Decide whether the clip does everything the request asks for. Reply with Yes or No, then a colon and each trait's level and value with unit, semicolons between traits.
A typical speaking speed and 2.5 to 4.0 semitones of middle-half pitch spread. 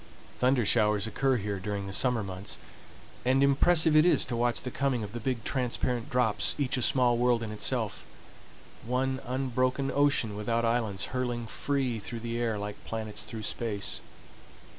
Yes: average, 160 wpm; average, 3.1 semitones